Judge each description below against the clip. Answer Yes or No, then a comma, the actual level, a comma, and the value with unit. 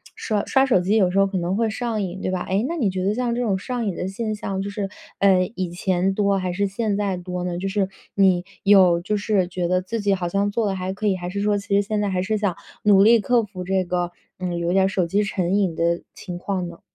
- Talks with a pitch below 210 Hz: Yes, high, 195 Hz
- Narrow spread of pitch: Yes, narrow, 2.2 semitones